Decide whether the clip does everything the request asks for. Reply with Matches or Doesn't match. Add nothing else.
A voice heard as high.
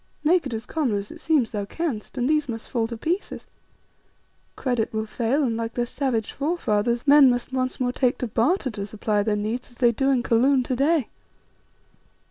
Matches